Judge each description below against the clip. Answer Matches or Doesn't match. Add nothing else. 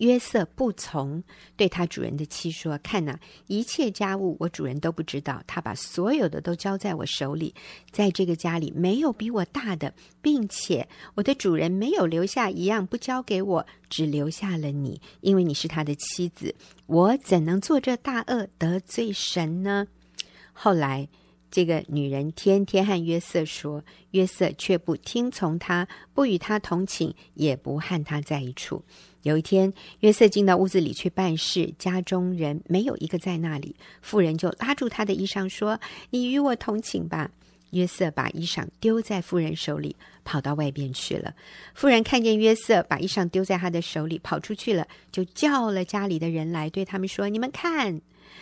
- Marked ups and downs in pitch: Doesn't match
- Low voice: Doesn't match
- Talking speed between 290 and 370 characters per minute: Doesn't match